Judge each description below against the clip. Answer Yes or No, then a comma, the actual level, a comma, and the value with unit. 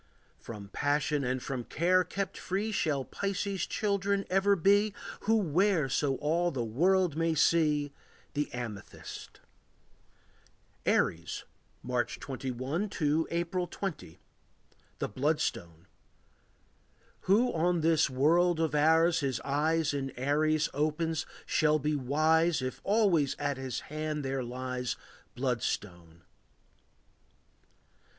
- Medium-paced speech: No, slow, 115 wpm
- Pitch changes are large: No, average, 4.6 semitones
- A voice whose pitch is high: No, medium, 155 Hz